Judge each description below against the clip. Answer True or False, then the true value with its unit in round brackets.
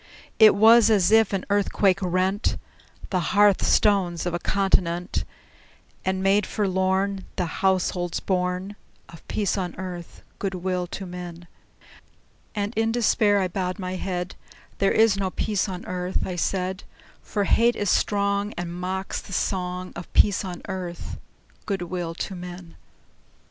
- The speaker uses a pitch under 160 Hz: False (190 Hz)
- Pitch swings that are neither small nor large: False (1.9 semitones)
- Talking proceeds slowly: False (150 wpm)